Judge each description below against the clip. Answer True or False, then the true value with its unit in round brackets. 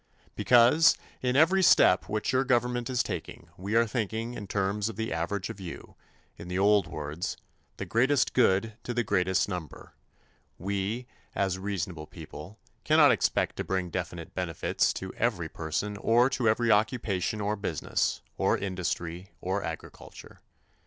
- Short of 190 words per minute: True (150 wpm)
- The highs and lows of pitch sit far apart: False (4.2 semitones)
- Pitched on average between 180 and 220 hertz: False (100 Hz)